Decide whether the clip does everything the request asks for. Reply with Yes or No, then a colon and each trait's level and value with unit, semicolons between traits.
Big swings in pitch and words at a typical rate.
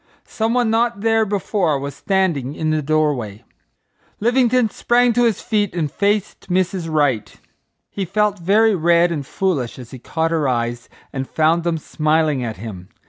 Yes: wide, 6.7 semitones; average, 165 wpm